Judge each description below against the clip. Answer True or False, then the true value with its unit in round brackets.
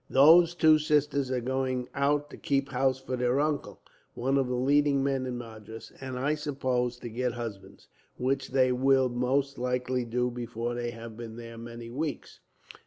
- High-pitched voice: False (130 Hz)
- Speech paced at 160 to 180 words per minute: True (175 wpm)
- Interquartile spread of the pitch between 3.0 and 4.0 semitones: False (2.4 semitones)